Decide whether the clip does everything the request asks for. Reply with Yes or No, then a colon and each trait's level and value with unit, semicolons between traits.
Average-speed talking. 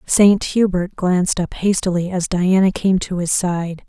Yes: average, 170 wpm